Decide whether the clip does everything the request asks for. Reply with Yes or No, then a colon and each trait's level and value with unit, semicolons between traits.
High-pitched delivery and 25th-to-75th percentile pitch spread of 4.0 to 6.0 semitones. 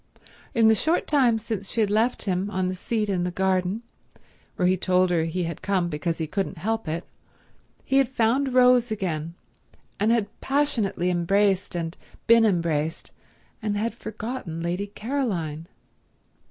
Yes: high, 200 Hz; average, 4.5 semitones